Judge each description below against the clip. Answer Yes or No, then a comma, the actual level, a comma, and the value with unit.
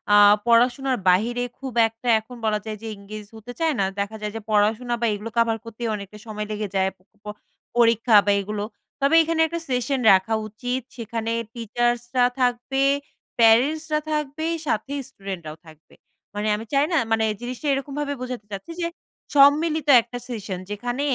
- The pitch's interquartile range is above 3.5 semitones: Yes, average, 4.0 semitones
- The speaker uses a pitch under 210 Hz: No, high, 235 Hz